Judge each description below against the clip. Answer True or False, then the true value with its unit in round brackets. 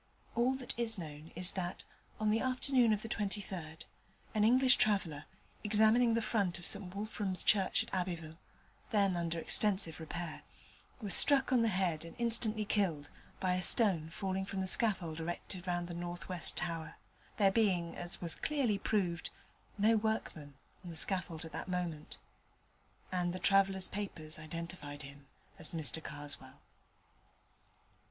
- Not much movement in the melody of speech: False (4.2 semitones)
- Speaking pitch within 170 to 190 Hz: True (185 Hz)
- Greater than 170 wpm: False (155 wpm)